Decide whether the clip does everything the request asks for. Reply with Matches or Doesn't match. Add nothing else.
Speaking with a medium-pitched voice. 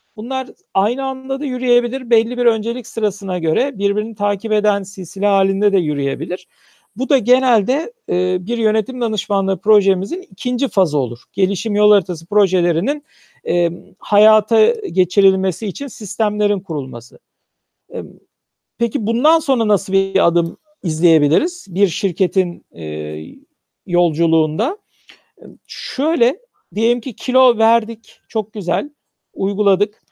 Doesn't match